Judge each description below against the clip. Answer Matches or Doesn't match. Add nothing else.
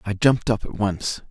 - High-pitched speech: Doesn't match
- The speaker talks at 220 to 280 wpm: Matches